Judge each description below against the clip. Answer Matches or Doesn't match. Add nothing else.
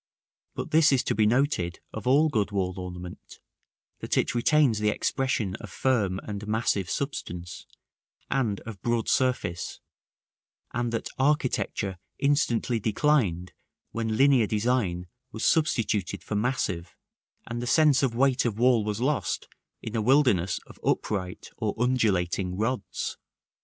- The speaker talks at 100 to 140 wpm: Matches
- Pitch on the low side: Matches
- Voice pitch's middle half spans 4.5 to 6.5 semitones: Matches